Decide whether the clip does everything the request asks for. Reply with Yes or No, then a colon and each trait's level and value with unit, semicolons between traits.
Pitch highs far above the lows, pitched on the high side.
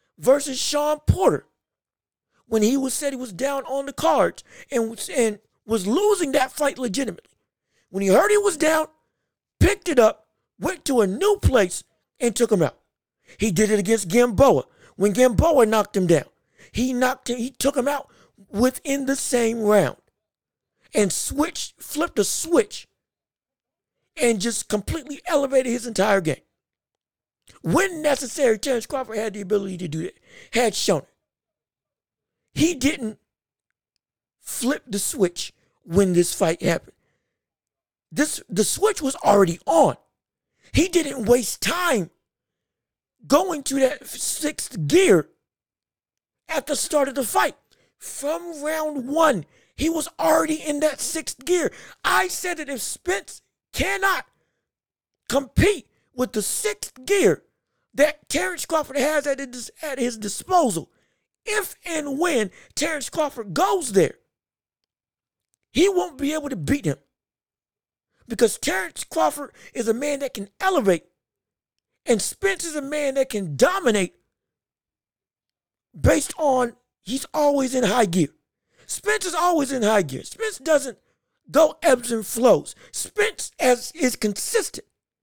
Yes: wide, 5.7 semitones; very high, 275 Hz